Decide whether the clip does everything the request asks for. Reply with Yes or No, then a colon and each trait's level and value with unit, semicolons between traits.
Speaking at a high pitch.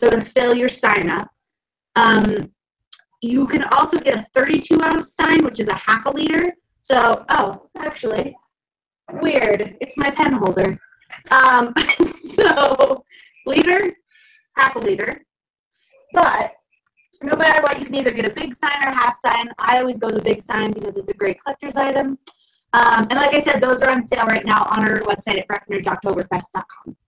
Yes: very high, 270 Hz